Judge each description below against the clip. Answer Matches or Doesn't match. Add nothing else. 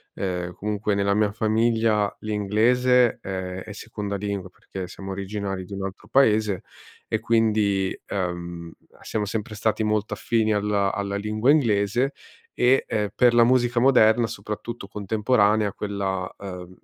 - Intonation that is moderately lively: Doesn't match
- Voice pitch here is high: Doesn't match